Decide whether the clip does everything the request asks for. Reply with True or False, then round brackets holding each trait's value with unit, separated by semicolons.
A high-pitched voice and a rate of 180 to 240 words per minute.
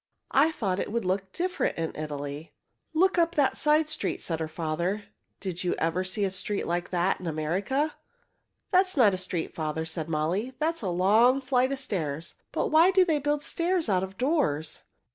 True (195 Hz; 200 wpm)